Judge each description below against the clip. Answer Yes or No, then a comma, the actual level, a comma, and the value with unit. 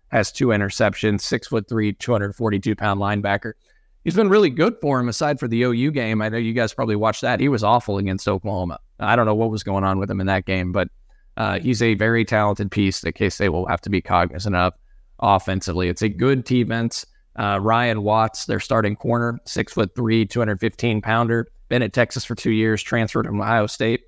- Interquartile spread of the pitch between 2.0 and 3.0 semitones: Yes, average, 2.7 semitones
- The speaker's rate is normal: No, fast, 225 wpm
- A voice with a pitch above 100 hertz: Yes, low, 110 Hz